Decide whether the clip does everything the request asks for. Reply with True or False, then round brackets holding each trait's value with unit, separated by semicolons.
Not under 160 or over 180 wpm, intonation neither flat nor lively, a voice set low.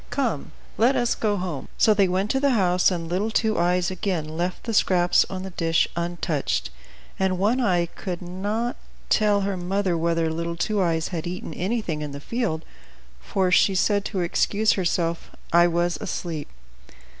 False (175 wpm; 3.2 semitones; 180 Hz)